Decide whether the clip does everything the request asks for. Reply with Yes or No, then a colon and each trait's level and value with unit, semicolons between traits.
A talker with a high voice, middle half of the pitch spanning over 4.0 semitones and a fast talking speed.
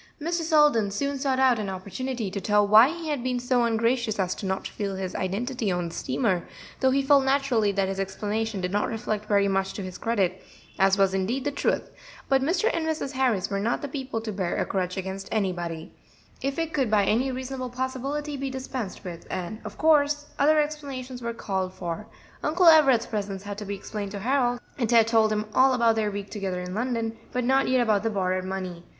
Yes: high, 225 Hz; average, 5.3 semitones; fast, 215 wpm